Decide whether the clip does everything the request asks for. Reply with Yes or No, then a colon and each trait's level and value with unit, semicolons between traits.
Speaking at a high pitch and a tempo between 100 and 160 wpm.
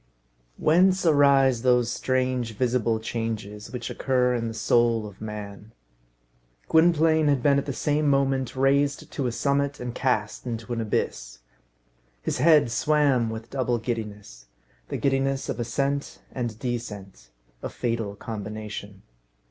No: low, 125 Hz; slow, 135 wpm